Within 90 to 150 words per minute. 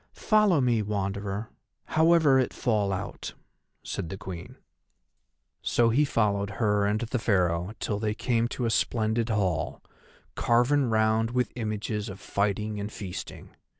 Yes: average, 140 wpm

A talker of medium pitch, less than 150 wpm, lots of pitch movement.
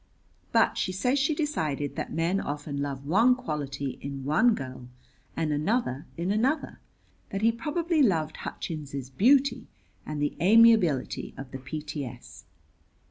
Yes: medium, 160 Hz; slow, 135 wpm; wide, 8.6 semitones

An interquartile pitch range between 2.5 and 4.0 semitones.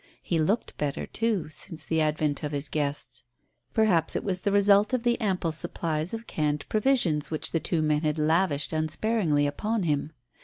No: average, 5.1 semitones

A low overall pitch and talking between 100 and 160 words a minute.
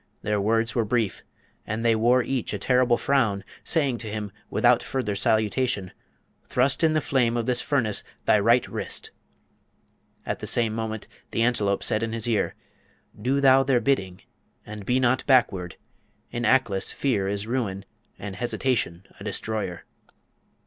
Yes: low, 115 Hz; average, 155 wpm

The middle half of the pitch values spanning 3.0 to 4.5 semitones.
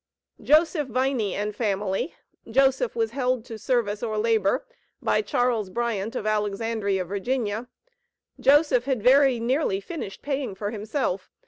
Yes: average, 4.2 semitones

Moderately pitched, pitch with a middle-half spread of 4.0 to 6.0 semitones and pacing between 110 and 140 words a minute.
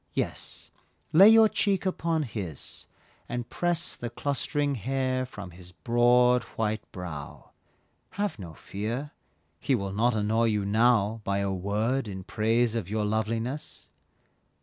No: low, 115 Hz; average, 4.6 semitones; slow, 135 wpm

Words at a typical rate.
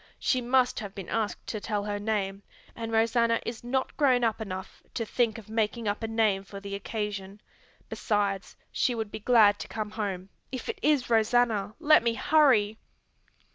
Yes: average, 180 wpm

